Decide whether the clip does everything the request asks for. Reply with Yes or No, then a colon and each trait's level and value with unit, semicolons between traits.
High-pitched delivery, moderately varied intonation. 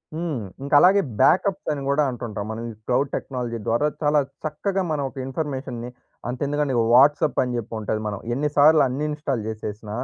No: low, 135 Hz; average, 4.1 semitones